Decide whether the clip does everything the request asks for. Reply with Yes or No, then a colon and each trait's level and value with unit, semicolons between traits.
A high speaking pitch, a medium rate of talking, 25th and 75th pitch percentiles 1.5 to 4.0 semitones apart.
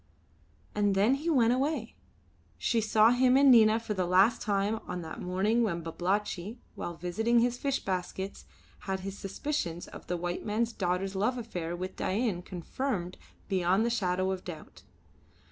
No: high, 200 Hz; average, 160 wpm; average, 4.4 semitones